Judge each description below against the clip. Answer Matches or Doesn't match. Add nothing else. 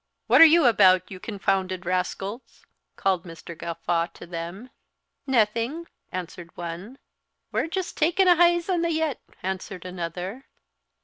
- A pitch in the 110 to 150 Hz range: Doesn't match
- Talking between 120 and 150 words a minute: Matches